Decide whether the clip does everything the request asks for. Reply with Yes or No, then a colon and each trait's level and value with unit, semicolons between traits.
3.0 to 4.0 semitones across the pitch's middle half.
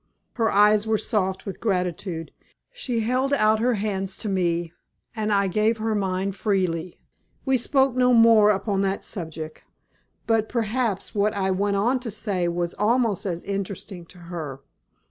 Yes: average, 3.3 semitones